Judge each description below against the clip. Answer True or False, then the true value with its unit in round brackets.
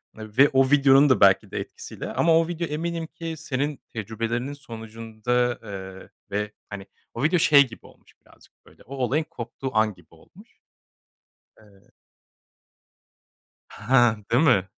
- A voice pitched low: True (125 Hz)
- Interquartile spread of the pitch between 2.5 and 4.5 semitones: False (4.9 semitones)